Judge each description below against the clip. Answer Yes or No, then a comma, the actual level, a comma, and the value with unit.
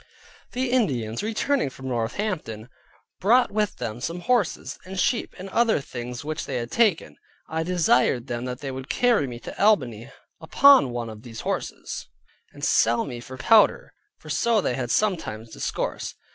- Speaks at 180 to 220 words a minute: No, average, 165 wpm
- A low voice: No, medium, 145 Hz